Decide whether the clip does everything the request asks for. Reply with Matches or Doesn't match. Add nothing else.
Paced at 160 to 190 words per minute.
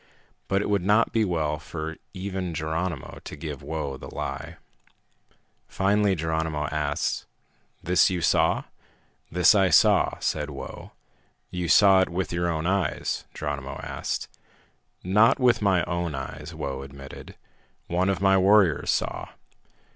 Doesn't match